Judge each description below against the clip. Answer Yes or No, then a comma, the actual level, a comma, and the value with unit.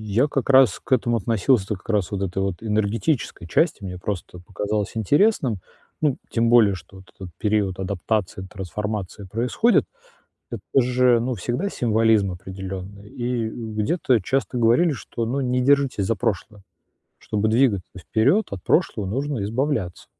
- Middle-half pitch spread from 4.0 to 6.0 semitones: Yes, average, 4.3 semitones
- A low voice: Yes, low, 110 Hz